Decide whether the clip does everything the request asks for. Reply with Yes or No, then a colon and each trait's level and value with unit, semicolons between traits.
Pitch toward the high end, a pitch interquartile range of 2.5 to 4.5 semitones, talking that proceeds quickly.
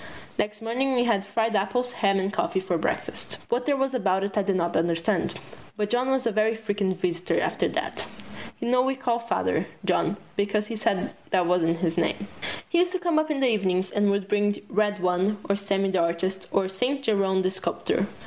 Yes: high, 205 Hz; average, 4.1 semitones; fast, 215 wpm